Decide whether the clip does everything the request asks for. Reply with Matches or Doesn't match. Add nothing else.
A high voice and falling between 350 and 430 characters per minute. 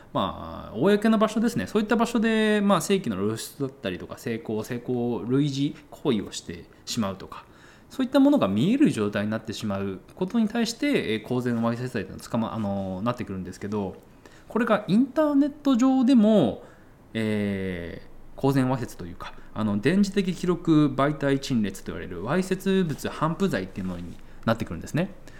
Doesn't match